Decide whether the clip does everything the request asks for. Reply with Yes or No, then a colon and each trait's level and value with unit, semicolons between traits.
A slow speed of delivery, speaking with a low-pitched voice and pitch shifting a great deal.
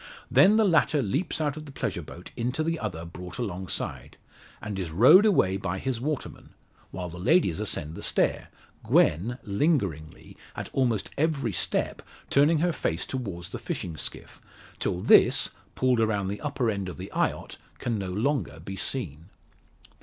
No: average, 165 wpm; low, 110 Hz; wide, 7.7 semitones